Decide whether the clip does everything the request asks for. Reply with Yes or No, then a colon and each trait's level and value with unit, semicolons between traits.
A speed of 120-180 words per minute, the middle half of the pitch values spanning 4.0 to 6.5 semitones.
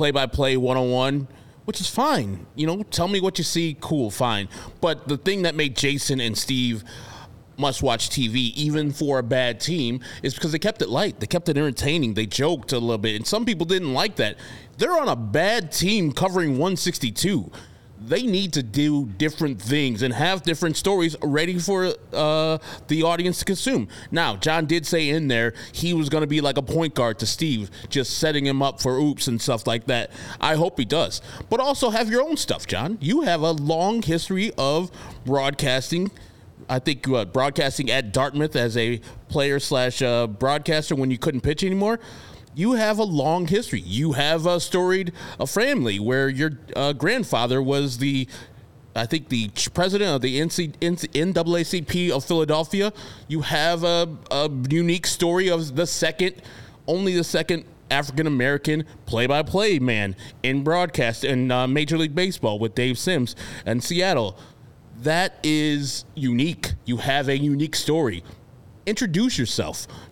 Yes: average, 175 wpm; average, 5.2 semitones